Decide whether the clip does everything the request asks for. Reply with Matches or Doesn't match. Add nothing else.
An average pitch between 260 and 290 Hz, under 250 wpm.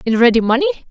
Matches